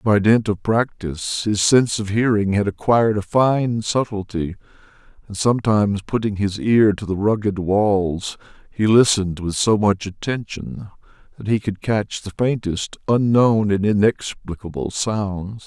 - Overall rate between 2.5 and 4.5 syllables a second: Yes, 4.4 syllables/s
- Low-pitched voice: Yes, low, 105 Hz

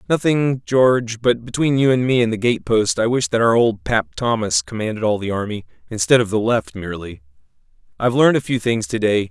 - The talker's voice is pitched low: Yes, low, 115 Hz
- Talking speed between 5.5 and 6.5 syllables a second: Yes, 5.7 syllables/s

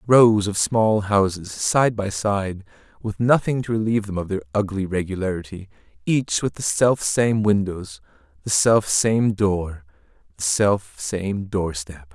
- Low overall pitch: Yes, low, 100 Hz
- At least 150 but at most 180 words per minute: Yes, average, 155 wpm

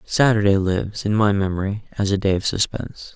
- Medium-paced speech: Yes, average, 190 wpm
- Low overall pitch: Yes, low, 100 Hz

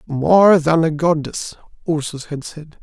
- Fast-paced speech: No, average, 150 wpm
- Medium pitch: Yes, medium, 155 Hz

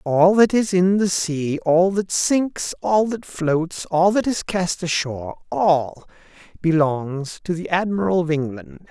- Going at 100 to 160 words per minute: Yes, average, 155 wpm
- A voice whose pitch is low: No, medium, 175 Hz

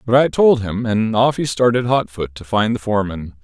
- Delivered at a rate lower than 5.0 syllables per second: No, 5.2 syllables/s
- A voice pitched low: Yes, low, 110 Hz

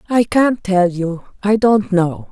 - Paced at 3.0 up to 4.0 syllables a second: Yes, 3.5 syllables/s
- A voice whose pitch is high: Yes, high, 195 Hz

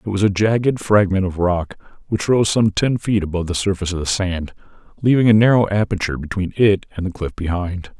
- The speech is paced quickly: Yes, fast, 210 wpm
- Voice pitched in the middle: No, low, 100 Hz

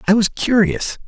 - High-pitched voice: Yes, high, 195 Hz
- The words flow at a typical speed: Yes, average, 165 wpm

